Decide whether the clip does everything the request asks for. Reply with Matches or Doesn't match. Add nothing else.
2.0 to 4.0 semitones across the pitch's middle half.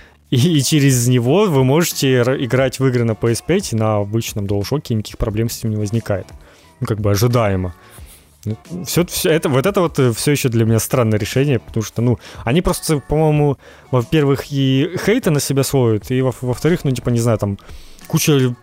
Doesn't match